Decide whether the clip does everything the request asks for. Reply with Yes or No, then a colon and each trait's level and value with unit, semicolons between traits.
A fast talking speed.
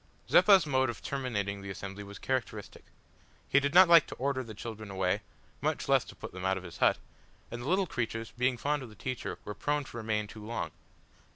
Yes: fast, 215 wpm